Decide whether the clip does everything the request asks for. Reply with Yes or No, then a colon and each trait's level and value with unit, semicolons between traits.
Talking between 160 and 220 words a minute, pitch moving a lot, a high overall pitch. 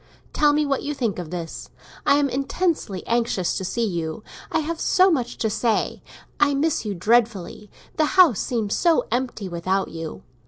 Yes: average, 180 wpm; wide, 7.4 semitones; high, 235 Hz